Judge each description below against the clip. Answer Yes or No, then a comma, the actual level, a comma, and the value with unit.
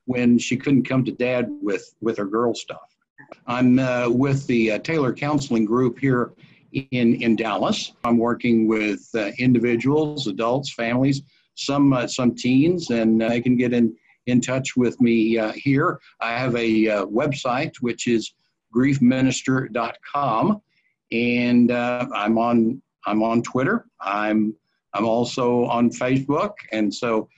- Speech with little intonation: Yes, narrow, 2.3 semitones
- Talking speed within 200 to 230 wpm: No, average, 145 wpm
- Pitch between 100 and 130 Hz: Yes, low, 120 Hz